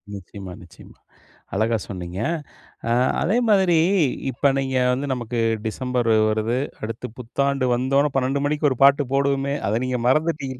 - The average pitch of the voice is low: Yes, low, 130 Hz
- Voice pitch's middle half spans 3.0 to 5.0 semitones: Yes, average, 3.5 semitones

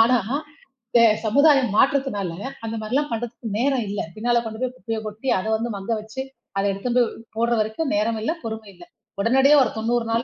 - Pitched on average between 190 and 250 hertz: Yes, high, 230 Hz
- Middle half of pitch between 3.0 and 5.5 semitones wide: No, narrow, 2.6 semitones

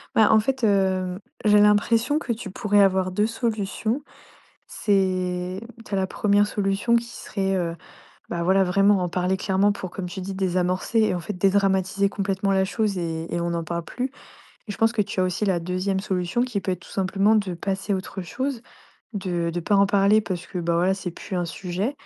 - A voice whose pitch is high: Yes, high, 195 Hz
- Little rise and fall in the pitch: Yes, narrow, 2.3 semitones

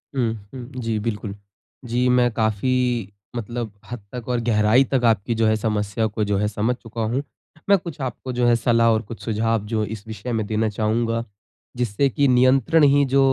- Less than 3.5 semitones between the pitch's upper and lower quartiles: Yes, narrow, 2.4 semitones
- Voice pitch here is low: Yes, low, 115 Hz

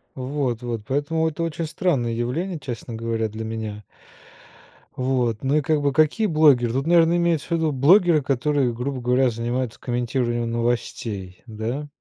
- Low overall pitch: Yes, low, 130 Hz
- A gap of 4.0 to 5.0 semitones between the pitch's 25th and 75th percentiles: Yes, average, 4.6 semitones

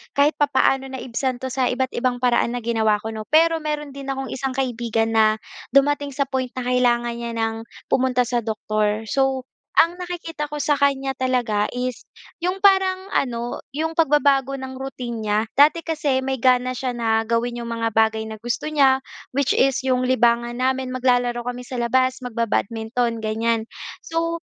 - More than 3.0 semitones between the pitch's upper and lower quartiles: No, average, 2.7 semitones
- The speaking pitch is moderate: No, very high, 255 Hz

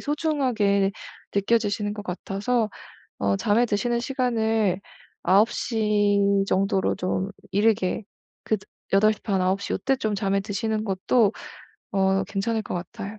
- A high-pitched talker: Yes, high, 205 Hz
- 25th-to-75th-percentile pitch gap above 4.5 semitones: No, narrow, 2.4 semitones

